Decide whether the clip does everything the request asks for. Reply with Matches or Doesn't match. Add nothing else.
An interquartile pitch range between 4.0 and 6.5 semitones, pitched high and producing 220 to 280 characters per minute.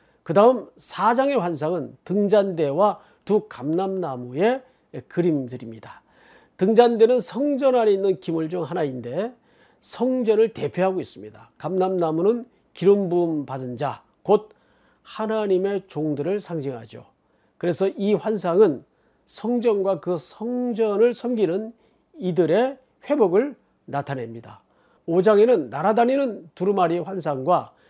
Matches